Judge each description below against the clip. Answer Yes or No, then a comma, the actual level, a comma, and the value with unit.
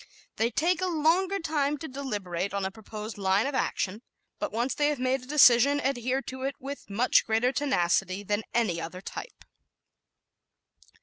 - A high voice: Yes, very high, 250 Hz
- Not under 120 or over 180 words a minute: Yes, average, 170 wpm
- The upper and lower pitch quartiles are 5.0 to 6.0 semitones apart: Yes, wide, 5.6 semitones